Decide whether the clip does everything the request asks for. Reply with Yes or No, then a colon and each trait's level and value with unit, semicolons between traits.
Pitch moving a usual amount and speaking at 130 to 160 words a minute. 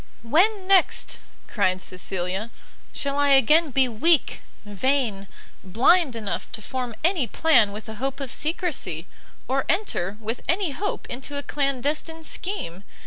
No: wide, 7.0 semitones; average, 140 wpm